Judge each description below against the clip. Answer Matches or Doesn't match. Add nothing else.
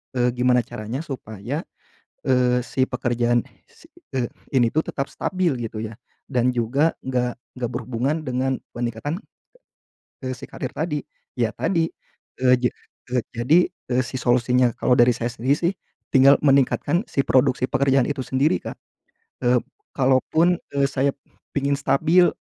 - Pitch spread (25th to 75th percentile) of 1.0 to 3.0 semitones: Matches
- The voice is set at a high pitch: Doesn't match